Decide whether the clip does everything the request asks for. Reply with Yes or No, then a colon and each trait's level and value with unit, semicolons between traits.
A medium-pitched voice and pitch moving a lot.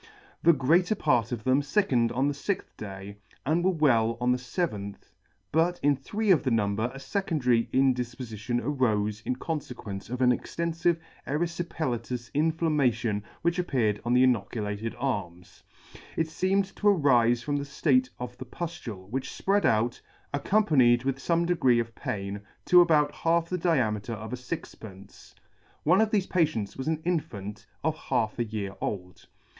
No: low, 130 Hz; wide, 6.2 semitones